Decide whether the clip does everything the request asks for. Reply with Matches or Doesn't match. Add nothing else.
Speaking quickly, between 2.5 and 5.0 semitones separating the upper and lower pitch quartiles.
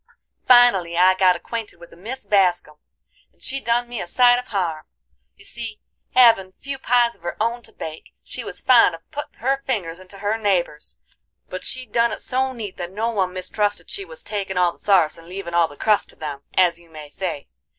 Doesn't match